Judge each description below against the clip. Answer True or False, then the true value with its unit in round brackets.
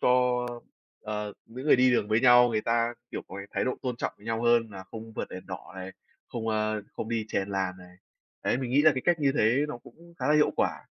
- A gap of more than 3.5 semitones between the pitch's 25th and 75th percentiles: False (2.9 semitones)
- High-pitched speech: False (115 Hz)